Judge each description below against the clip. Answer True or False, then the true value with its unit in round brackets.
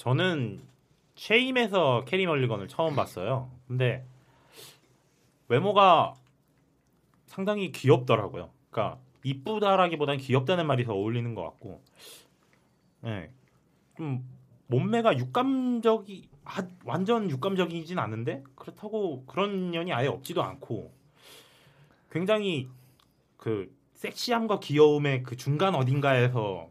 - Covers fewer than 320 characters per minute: True (250 characters per minute)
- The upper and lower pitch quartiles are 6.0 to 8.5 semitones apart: True (6.7 semitones)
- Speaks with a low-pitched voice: False (145 Hz)